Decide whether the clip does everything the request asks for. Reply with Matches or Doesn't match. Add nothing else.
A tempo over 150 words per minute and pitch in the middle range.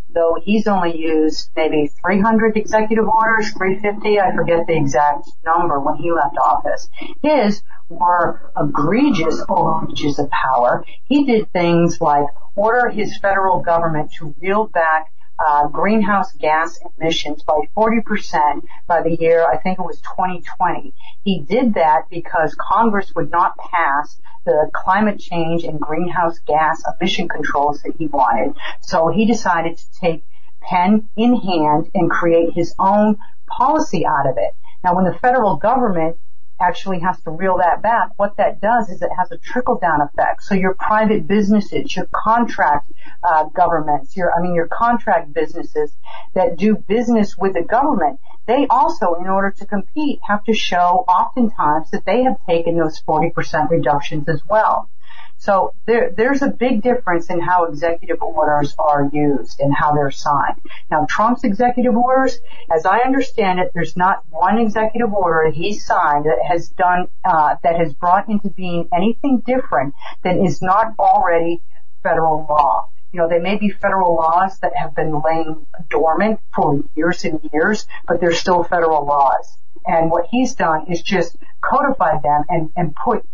Matches